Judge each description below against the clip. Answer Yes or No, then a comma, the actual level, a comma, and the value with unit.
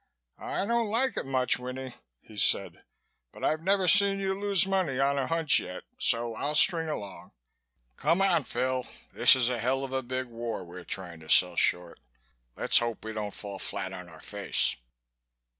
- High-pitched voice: No, low, 130 Hz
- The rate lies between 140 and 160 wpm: No, average, 190 wpm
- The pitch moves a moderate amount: No, wide, 7.5 semitones